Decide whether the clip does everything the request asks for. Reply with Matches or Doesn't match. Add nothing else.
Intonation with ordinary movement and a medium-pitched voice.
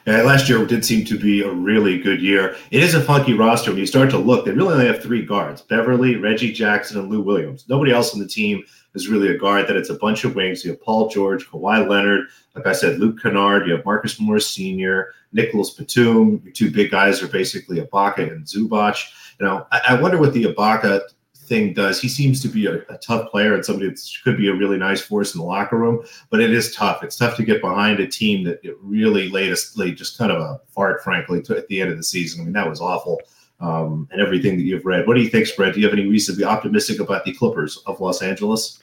Doesn't match